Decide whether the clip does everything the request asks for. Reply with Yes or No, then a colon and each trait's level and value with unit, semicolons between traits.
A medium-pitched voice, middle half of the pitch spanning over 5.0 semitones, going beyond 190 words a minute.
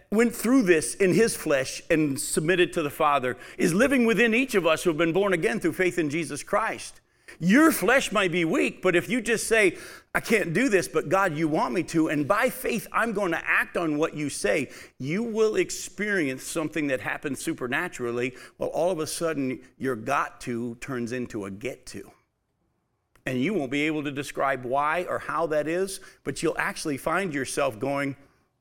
Yes: medium, 160 Hz; wide, 5.4 semitones; average, 200 wpm